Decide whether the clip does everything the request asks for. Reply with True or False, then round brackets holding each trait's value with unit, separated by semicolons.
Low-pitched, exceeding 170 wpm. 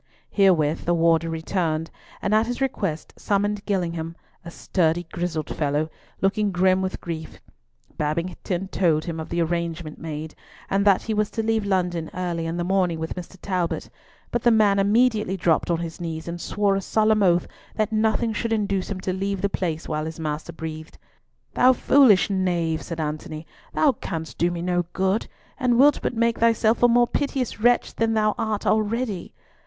False (185 Hz; 180 wpm)